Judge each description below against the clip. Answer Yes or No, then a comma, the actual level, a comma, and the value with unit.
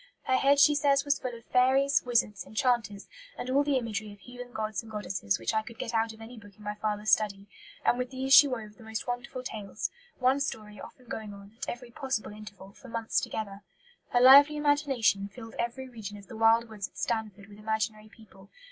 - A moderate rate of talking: No, fast, 215 wpm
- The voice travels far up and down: No, average, 3.3 semitones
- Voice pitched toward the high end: Yes, high, 225 Hz